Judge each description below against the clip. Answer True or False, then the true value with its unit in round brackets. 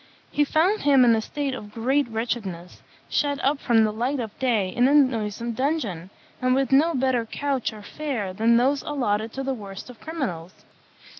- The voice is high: True (245 Hz)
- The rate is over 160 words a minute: True (190 wpm)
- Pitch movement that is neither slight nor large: True (4.3 semitones)